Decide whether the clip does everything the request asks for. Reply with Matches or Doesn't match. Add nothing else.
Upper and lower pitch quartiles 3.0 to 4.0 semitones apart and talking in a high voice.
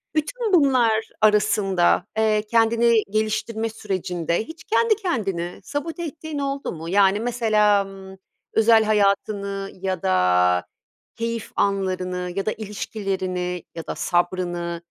Matches